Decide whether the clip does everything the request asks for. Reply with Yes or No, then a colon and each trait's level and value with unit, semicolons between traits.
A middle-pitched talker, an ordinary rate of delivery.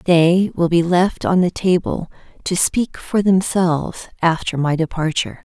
Yes: medium, 175 Hz; average, 150 wpm